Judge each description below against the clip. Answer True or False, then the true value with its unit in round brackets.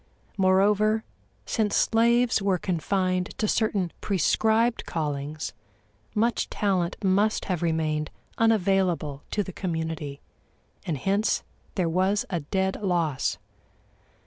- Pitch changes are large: False (4.3 semitones)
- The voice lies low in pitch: False (190 Hz)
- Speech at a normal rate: False (105 wpm)